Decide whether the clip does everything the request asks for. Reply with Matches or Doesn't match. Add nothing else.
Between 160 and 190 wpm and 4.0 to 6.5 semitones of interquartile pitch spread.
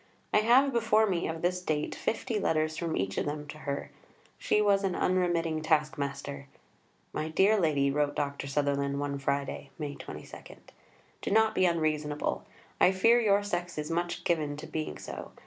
Matches